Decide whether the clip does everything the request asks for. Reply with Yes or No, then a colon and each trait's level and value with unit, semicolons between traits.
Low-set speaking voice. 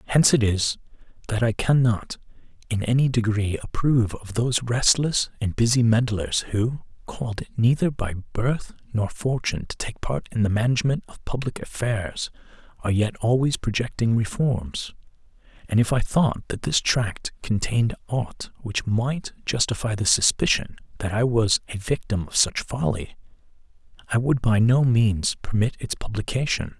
Yes: low, 115 Hz